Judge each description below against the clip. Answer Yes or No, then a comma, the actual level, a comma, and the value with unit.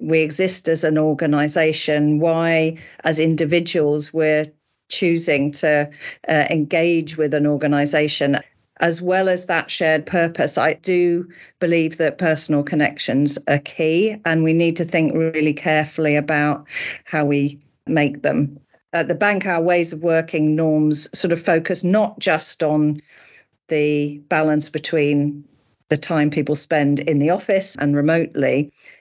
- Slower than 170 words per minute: Yes, average, 140 wpm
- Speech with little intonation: Yes, narrow, 2.0 semitones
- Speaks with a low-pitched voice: No, medium, 155 Hz